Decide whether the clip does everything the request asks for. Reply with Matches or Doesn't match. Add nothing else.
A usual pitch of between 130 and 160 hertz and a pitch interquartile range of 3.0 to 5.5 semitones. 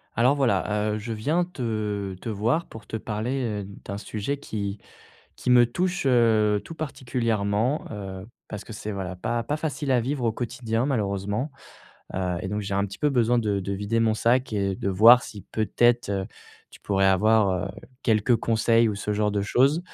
Doesn't match